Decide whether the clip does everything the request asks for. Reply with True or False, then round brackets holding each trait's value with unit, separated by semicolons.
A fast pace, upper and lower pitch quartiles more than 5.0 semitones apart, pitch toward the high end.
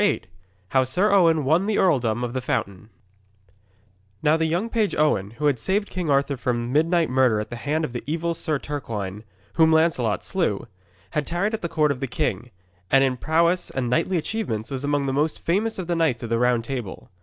False (210 wpm; 5.4 semitones; 145 Hz)